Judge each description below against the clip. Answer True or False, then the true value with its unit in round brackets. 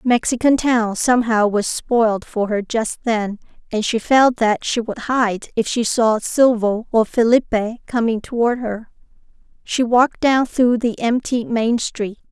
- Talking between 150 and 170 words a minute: True (160 wpm)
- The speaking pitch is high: True (230 Hz)